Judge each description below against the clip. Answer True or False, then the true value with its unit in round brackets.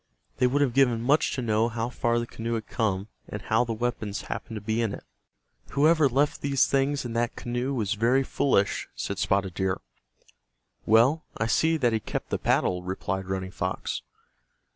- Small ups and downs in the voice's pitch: False (4.2 semitones)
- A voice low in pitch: True (115 Hz)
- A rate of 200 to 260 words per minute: False (185 wpm)